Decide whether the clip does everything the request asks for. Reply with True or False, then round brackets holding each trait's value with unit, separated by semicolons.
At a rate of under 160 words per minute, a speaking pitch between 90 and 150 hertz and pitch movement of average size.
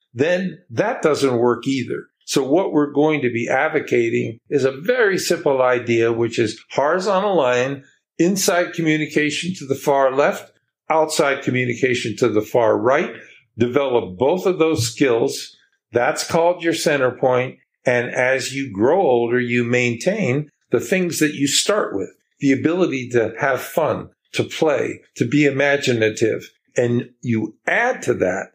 True (150 wpm; 135 Hz; 4.0 semitones)